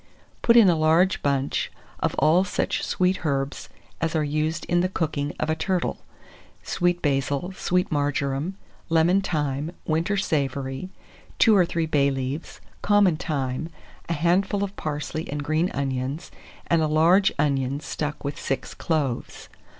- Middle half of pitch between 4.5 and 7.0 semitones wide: No, average, 3.8 semitones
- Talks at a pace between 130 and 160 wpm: Yes, average, 150 wpm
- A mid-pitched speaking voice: Yes, medium, 155 Hz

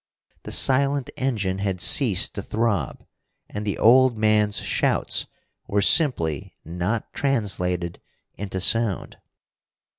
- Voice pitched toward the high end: No, low, 105 Hz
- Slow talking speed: Yes, slow, 110 wpm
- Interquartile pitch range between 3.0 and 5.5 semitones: Yes, average, 4.3 semitones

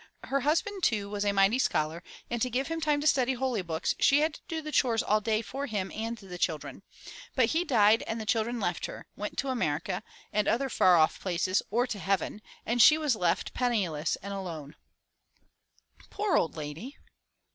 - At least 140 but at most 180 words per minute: No, average, 200 wpm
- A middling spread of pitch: No, wide, 5.8 semitones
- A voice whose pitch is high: Yes, high, 225 Hz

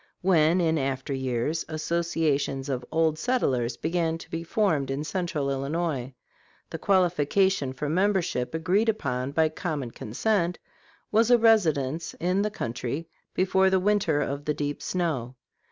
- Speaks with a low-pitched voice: No, medium, 160 Hz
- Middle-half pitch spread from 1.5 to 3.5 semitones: No, average, 4.9 semitones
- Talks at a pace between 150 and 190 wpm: No, average, 140 wpm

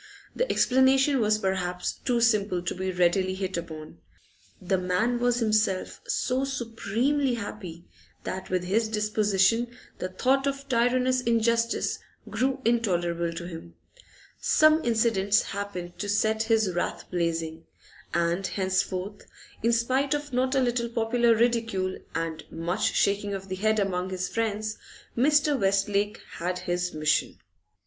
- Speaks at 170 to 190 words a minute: No, slow, 135 wpm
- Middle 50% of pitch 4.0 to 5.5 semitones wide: Yes, average, 4.6 semitones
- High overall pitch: Yes, high, 210 Hz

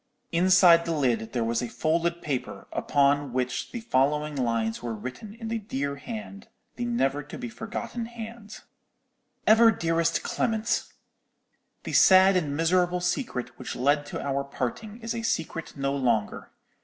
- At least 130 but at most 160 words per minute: Yes, average, 150 wpm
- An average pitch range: No, wide, 7.9 semitones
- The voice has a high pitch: No, medium, 165 Hz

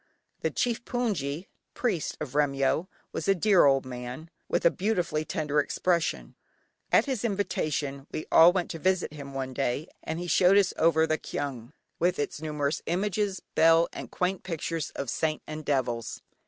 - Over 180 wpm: No, average, 170 wpm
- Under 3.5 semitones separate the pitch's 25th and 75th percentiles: No, average, 4.4 semitones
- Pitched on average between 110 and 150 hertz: No, medium, 160 Hz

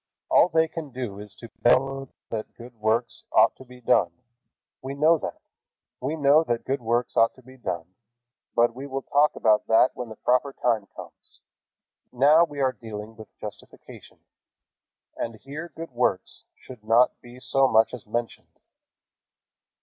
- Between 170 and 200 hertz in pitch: No, low, 125 Hz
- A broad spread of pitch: No, average, 3.3 semitones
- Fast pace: No, average, 165 wpm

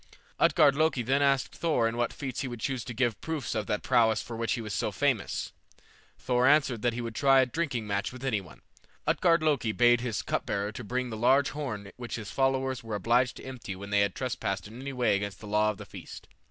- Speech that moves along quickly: Yes, fast, 235 wpm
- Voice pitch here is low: Yes, low, 120 Hz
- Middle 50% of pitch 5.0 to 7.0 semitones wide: No, average, 3.7 semitones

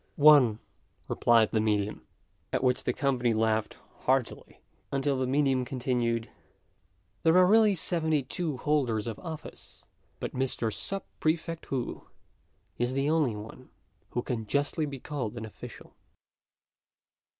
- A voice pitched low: Yes, low, 130 Hz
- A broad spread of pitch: No, average, 4.4 semitones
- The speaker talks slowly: Yes, slow, 130 wpm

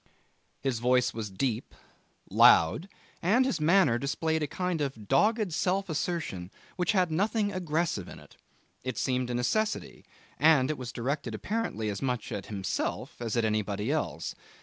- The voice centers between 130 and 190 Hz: Yes, medium, 140 Hz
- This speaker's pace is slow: No, average, 155 wpm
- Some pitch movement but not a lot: No, wide, 7.7 semitones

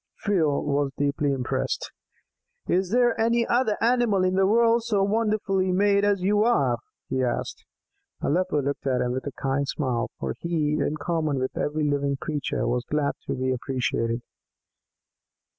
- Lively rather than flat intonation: Yes, wide, 6.6 semitones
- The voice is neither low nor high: Yes, medium, 155 Hz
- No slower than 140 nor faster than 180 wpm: Yes, average, 160 wpm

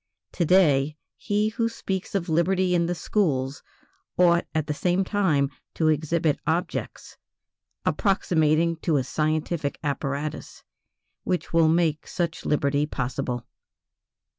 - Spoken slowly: Yes, slow, 120 wpm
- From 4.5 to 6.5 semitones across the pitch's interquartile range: No, average, 3.4 semitones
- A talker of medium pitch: Yes, medium, 160 Hz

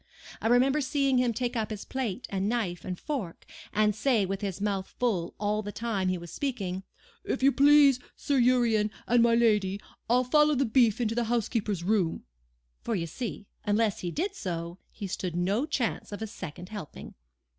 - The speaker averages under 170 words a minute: No, average, 190 wpm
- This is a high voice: Yes, high, 220 Hz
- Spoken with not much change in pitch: No, average, 4.3 semitones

